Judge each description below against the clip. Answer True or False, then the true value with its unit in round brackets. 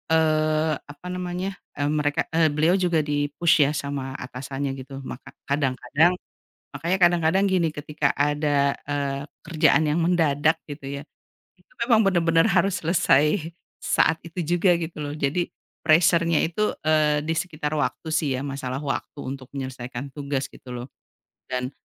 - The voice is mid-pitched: True (150 Hz)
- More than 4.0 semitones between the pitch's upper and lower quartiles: False (3.1 semitones)